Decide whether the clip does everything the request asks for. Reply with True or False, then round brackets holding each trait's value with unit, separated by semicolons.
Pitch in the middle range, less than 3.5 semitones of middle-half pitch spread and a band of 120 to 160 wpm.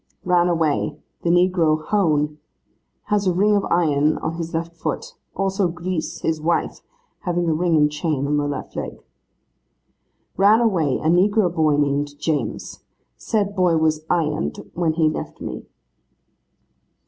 True (165 Hz; 2.8 semitones; 150 wpm)